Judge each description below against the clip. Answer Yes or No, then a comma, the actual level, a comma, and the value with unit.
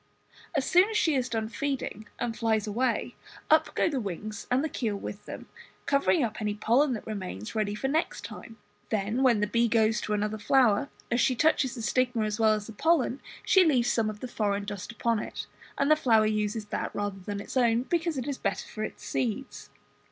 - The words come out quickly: Yes, fast, 215 wpm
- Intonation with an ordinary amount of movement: Yes, average, 4.0 semitones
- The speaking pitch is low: No, high, 225 Hz